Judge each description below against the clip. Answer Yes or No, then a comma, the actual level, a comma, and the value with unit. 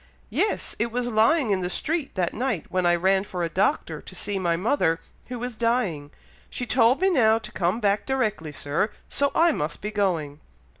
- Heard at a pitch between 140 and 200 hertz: No, high, 210 Hz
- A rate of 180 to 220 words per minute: Yes, average, 200 wpm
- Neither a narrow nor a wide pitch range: No, wide, 5.9 semitones